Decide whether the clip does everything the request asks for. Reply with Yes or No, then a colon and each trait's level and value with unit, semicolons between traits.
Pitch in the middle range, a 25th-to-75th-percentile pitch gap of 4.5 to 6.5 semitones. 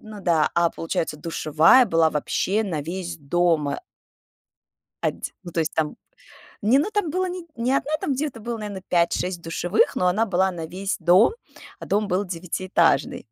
Yes: medium, 180 Hz; average, 4.9 semitones